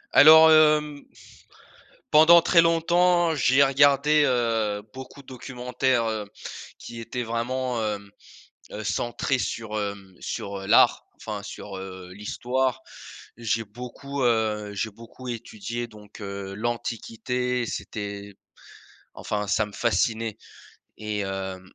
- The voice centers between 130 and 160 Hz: No, low, 115 Hz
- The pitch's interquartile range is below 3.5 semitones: No, average, 4.1 semitones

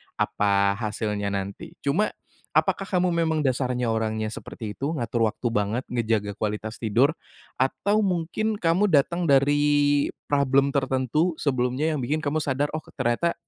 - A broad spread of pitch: Yes, wide, 5.8 semitones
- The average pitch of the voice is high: No, low, 135 Hz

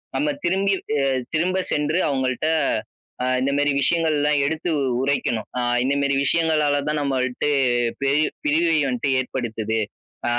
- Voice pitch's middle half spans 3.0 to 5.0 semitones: Yes, average, 3.3 semitones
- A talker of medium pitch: Yes, medium, 145 Hz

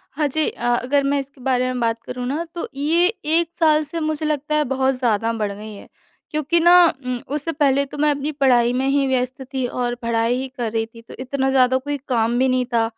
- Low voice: No, very high, 265 Hz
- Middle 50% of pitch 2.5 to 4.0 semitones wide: Yes, average, 3.5 semitones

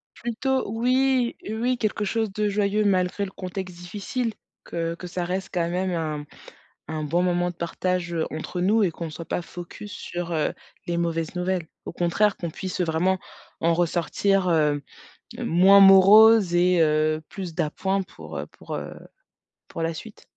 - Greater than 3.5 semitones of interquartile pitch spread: No, average, 3.2 semitones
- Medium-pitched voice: Yes, medium, 180 Hz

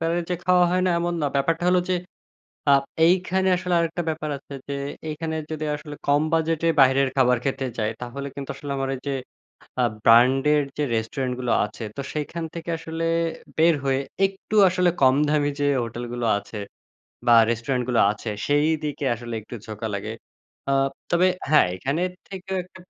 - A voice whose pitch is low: No, medium, 150 Hz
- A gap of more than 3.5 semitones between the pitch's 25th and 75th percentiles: Yes, average, 4.5 semitones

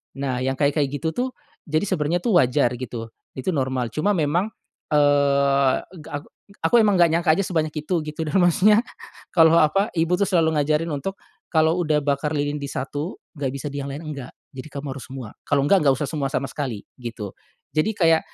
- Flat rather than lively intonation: No, average, 3.3 semitones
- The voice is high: No, medium, 150 Hz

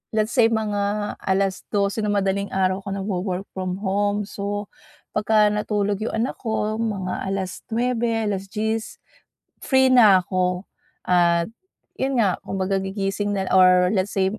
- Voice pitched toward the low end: No, high, 200 Hz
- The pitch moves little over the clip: Yes, narrow, 2.0 semitones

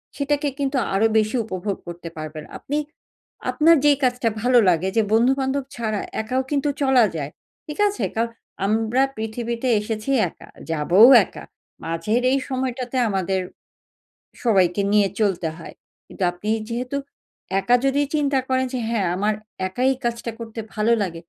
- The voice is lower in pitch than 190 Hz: No, high, 230 Hz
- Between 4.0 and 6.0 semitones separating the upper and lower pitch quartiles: Yes, average, 4.9 semitones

